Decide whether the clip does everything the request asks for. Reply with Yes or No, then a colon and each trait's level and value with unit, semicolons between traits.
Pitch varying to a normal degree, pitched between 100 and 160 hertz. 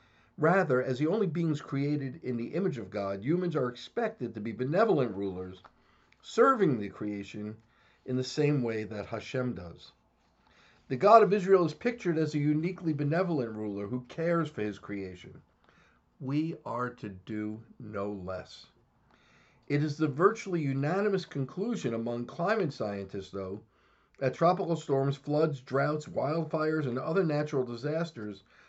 No: wide, 7.1 semitones; low, 135 Hz